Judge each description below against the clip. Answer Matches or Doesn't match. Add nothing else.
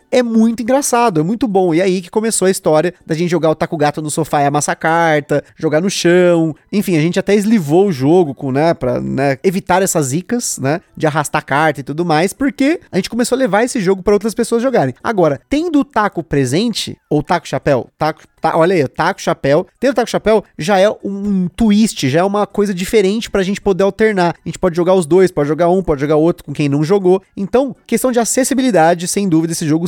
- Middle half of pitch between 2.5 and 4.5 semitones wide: Doesn't match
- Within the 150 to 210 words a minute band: Doesn't match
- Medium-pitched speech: Matches